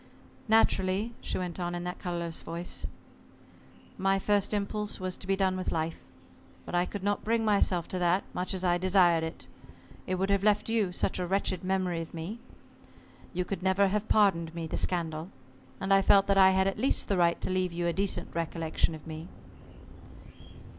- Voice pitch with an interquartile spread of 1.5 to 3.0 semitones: Yes, narrow, 2.4 semitones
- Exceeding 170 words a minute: Yes, average, 195 wpm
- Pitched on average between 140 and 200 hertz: Yes, medium, 185 Hz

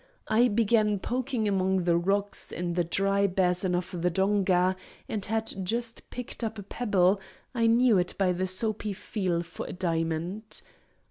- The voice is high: Yes, high, 195 Hz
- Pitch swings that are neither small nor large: Yes, average, 3.4 semitones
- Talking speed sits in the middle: Yes, average, 155 wpm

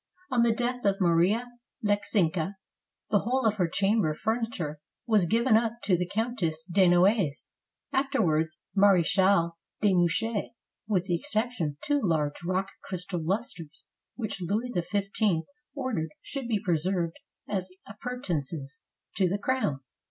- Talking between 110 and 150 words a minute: Yes, average, 140 wpm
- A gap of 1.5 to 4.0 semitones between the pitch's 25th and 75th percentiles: No, average, 4.8 semitones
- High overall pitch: Yes, high, 195 Hz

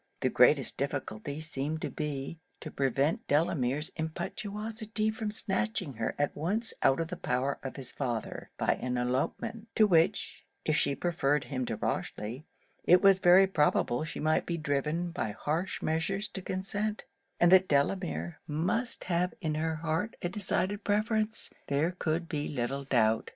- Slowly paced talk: No, average, 160 wpm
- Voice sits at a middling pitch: Yes, medium, 160 Hz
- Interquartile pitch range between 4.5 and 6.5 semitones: Yes, wide, 5.4 semitones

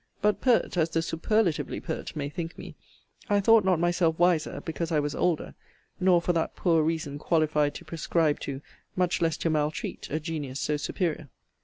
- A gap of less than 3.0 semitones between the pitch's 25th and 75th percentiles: Yes, narrow, 2.5 semitones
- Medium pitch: Yes, medium, 165 Hz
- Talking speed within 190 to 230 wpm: No, average, 180 wpm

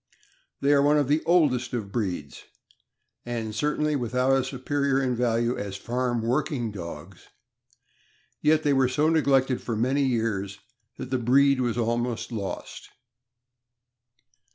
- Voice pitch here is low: Yes, low, 125 Hz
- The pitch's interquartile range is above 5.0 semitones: No, average, 3.4 semitones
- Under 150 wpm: Yes, average, 140 wpm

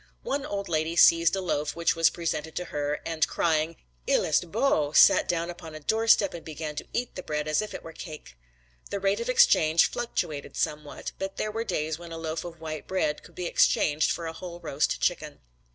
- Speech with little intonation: No, average, 3.3 semitones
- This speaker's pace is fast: Yes, fast, 215 wpm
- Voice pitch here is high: No, medium, 165 Hz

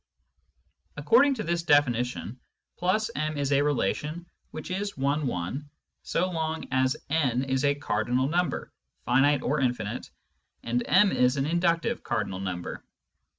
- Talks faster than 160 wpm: No, average, 145 wpm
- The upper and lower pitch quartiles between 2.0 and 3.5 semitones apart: No, average, 4.8 semitones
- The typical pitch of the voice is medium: Yes, medium, 145 Hz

